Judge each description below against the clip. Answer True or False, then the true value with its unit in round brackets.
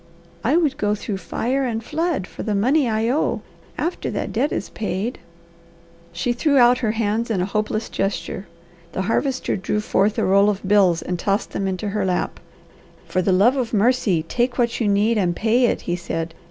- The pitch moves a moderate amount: True (4.3 semitones)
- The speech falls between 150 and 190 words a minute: False (200 wpm)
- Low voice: False (215 Hz)